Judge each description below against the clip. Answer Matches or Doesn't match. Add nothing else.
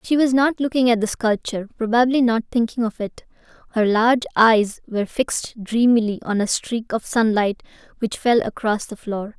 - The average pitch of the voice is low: Doesn't match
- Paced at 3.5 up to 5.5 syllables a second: Matches